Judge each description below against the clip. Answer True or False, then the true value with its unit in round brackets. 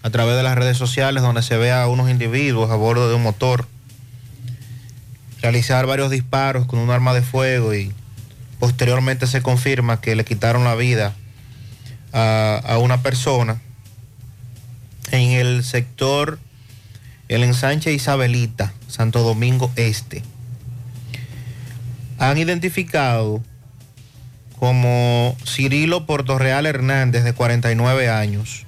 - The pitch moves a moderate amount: False (1.4 semitones)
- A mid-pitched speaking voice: False (125 Hz)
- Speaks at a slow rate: True (120 wpm)